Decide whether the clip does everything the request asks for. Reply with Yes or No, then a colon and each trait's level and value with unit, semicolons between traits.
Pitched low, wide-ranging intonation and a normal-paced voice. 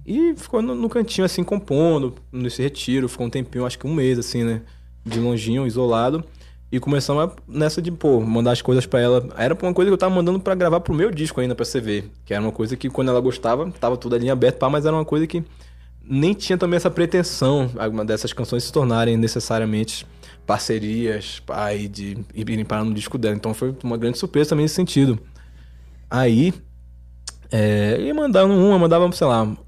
No: low, 125 Hz; wide, 6.3 semitones; fast, 200 wpm